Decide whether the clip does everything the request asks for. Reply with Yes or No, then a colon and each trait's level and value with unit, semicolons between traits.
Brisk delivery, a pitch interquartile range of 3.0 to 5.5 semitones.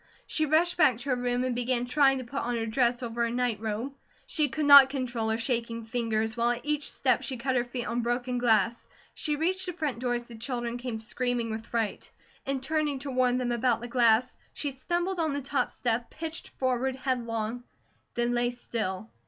No: fast, 210 wpm; narrow, 2.5 semitones